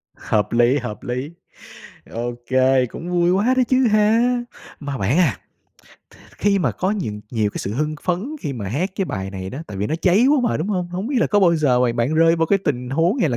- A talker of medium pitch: Yes, medium, 155 Hz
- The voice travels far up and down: Yes, wide, 8.1 semitones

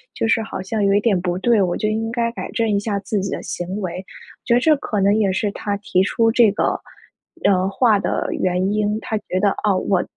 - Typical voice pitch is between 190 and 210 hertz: Yes, high, 205 Hz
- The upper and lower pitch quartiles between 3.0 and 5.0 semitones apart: No, narrow, 2.6 semitones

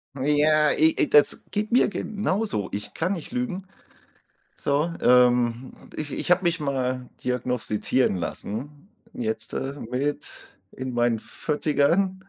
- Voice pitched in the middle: Yes, medium, 145 Hz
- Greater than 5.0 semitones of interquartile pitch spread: Yes, wide, 5.4 semitones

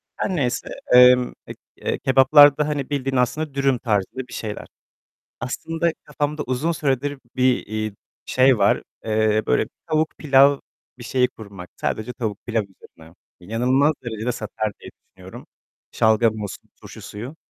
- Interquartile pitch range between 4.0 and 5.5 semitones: Yes, average, 4.3 semitones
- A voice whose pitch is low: Yes, low, 125 Hz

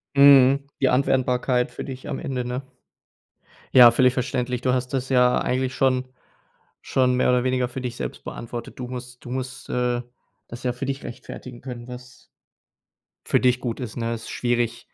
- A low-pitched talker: Yes, low, 125 Hz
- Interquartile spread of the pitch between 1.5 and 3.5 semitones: No, narrow, 0.9 semitones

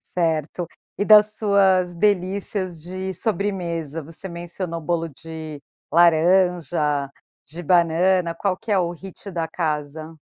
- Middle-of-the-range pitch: Yes, medium, 175 Hz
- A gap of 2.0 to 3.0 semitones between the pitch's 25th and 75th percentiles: Yes, average, 2.7 semitones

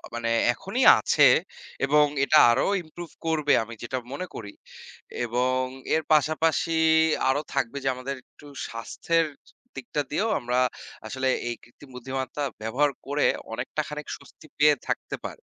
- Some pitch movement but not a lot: Yes, average, 3.5 semitones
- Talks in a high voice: No, medium, 140 Hz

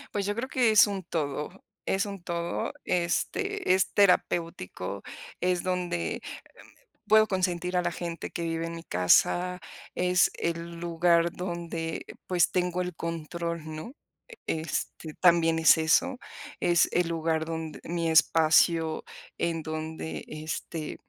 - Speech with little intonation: Yes, narrow, 1.9 semitones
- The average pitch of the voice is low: No, medium, 170 Hz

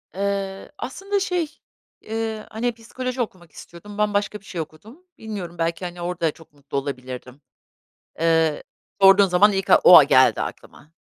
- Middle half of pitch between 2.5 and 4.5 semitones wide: No, average, 5.1 semitones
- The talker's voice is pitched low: No, high, 195 Hz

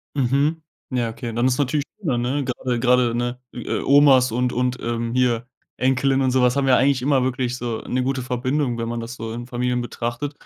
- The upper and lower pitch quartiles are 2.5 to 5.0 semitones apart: No, narrow, 1.8 semitones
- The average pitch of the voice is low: Yes, low, 125 Hz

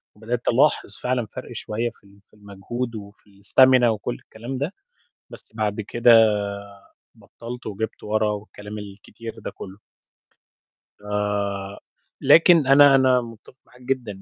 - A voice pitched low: Yes, low, 115 Hz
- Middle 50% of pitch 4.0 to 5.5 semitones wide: No, average, 3.4 semitones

